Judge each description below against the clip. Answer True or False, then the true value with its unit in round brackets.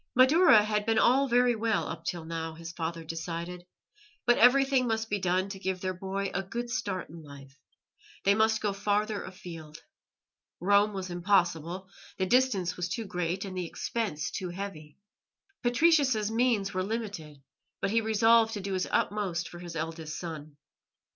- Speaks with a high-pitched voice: True (195 Hz)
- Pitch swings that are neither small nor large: True (4.5 semitones)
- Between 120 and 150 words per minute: False (165 wpm)